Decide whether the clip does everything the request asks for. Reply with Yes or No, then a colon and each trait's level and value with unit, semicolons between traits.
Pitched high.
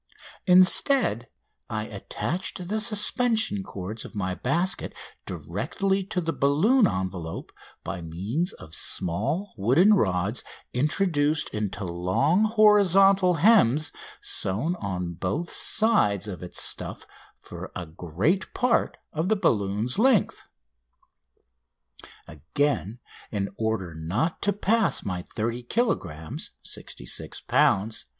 No: low, 135 Hz